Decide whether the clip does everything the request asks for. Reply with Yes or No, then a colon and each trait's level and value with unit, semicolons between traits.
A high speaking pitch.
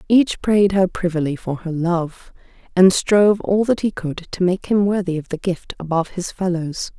No: medium, 180 Hz